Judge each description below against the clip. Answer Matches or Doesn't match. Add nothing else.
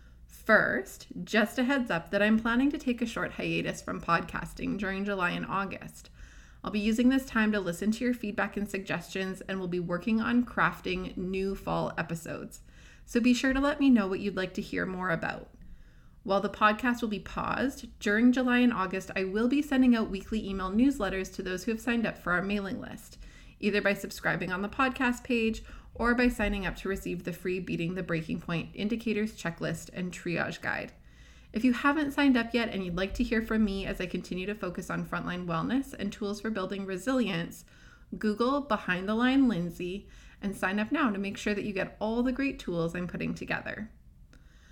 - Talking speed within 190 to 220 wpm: Matches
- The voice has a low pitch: Doesn't match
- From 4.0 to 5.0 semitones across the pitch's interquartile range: Matches